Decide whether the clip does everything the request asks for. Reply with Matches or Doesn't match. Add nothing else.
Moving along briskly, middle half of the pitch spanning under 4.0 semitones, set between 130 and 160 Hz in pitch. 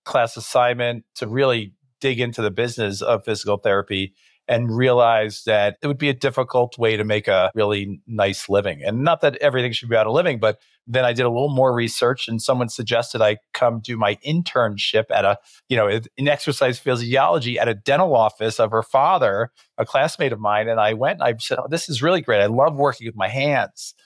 Doesn't match